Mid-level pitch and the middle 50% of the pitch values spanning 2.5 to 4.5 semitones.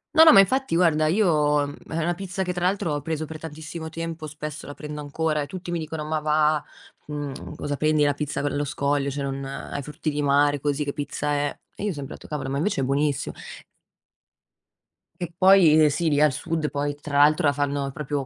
No: medium, 150 Hz; narrow, 2.1 semitones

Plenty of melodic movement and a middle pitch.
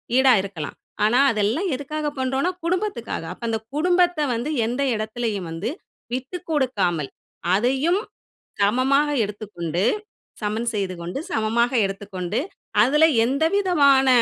No: wide, 6.1 semitones; high, 240 Hz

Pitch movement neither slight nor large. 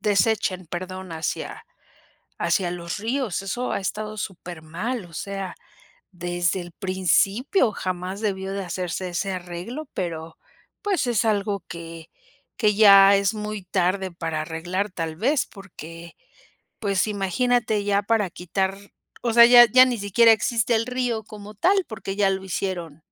Yes: average, 3.6 semitones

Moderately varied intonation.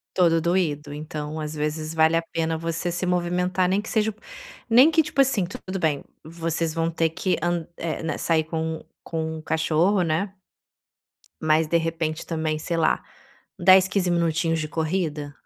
No: narrow, 2.2 semitones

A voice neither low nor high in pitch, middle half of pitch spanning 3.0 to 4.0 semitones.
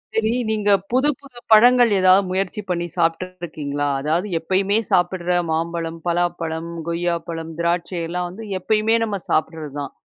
Yes: medium, 175 Hz; average, 3.6 semitones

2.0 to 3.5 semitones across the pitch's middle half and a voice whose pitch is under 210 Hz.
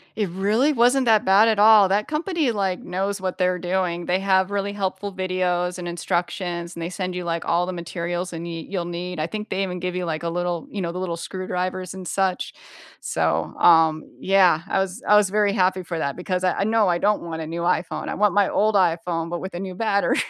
Yes: narrow, 2.4 semitones; medium, 185 Hz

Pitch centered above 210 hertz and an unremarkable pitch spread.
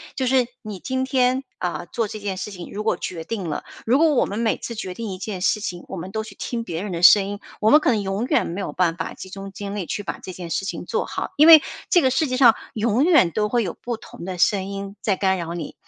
No: high, 205 Hz; average, 4.1 semitones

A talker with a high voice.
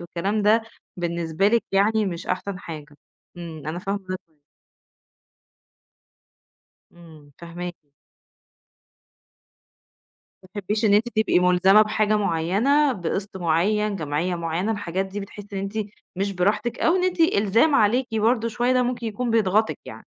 Yes: high, 200 Hz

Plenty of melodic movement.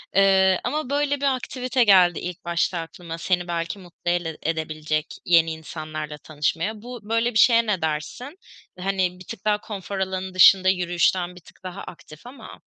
No: average, 4.1 semitones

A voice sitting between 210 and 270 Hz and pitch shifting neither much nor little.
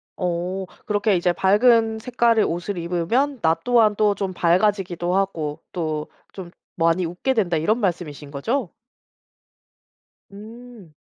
No: high, 190 Hz; average, 4.4 semitones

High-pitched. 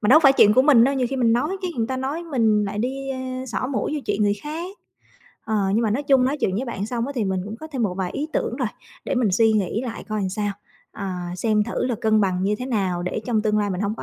Yes: high, 230 Hz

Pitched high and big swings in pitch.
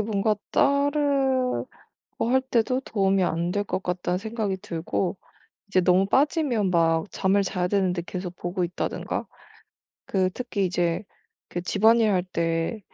No: high, 195 Hz; average, 3.8 semitones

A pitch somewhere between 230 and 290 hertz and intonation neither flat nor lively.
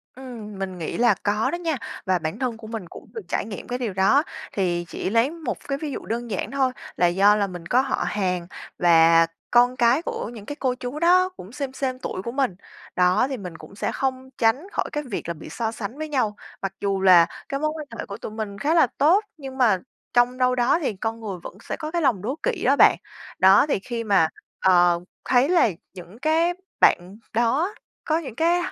No: high, 235 Hz; wide, 6.1 semitones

